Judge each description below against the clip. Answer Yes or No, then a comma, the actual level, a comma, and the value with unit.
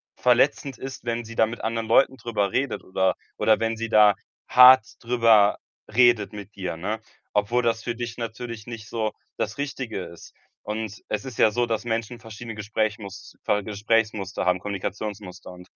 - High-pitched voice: No, low, 110 Hz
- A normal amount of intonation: No, narrow, 2.3 semitones